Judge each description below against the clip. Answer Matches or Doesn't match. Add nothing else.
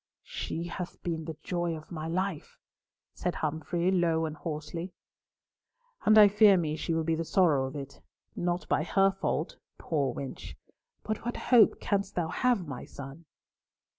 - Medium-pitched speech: Matches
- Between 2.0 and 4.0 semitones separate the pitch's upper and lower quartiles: Matches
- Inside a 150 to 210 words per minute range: Matches